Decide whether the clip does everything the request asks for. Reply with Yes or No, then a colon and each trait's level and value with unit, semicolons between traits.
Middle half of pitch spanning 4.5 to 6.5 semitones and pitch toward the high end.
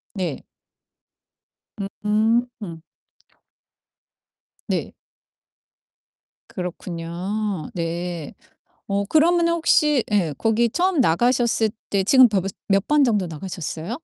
Yes: wide, 5.5 semitones; high, 205 Hz